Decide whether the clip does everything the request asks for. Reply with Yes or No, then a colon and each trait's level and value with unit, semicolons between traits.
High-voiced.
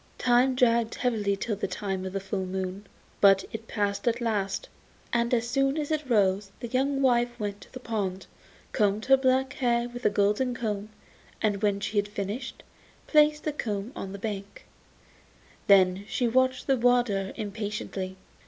Yes: high, 220 Hz